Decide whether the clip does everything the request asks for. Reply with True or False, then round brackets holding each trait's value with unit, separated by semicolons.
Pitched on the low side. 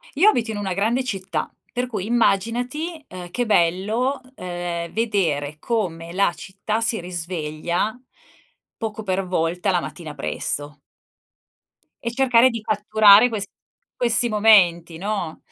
False (200 Hz)